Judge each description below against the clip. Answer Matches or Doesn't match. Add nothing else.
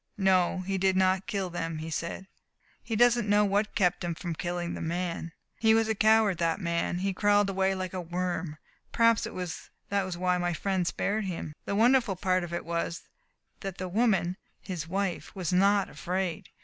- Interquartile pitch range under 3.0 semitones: Matches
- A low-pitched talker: Doesn't match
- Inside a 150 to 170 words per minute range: Doesn't match